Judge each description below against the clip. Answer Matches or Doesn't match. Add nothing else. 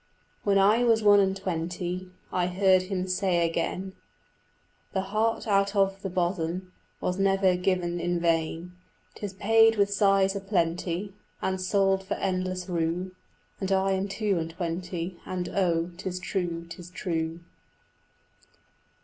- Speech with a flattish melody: Matches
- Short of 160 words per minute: Matches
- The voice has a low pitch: Doesn't match